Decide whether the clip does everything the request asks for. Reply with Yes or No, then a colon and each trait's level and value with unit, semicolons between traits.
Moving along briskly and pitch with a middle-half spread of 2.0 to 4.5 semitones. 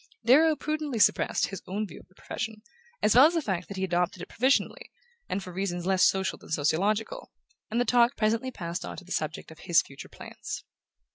No: fast, 215 wpm; wide, 5.4 semitones